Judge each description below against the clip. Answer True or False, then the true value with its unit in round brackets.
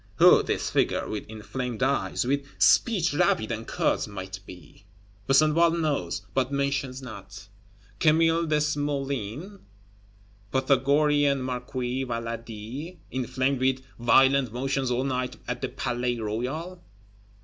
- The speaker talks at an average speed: False (115 wpm)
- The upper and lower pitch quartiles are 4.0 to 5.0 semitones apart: False (3.4 semitones)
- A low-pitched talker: True (130 Hz)